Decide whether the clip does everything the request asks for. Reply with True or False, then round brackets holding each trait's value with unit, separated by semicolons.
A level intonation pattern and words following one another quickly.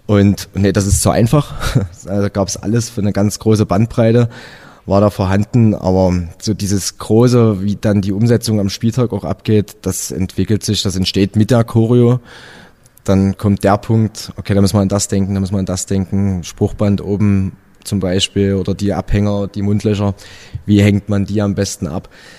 True (1.7 semitones; 195 wpm)